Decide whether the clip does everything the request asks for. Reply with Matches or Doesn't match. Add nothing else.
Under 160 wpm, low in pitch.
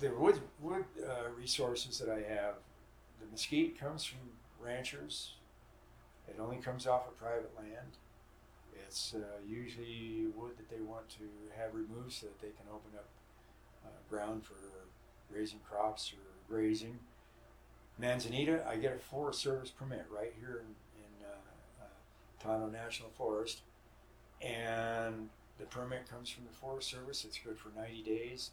Matches